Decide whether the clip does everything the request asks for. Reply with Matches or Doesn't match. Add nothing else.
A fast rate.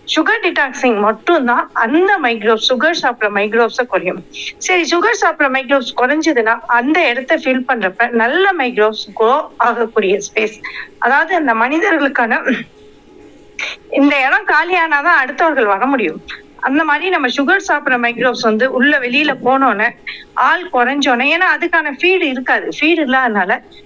Doesn't match